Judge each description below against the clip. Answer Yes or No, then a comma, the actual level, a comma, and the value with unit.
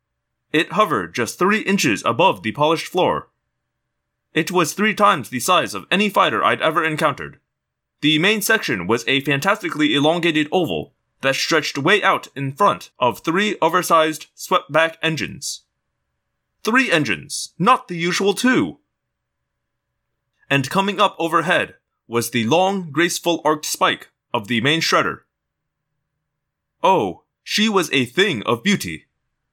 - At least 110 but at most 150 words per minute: Yes, average, 140 wpm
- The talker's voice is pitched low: No, medium, 165 Hz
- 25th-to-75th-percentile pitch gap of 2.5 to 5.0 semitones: No, wide, 5.6 semitones